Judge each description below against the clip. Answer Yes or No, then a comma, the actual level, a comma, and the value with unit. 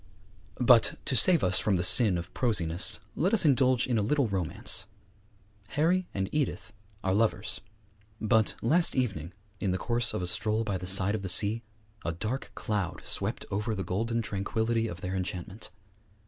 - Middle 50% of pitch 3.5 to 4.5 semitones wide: Yes, average, 4.2 semitones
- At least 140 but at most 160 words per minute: No, average, 175 wpm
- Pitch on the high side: No, low, 105 Hz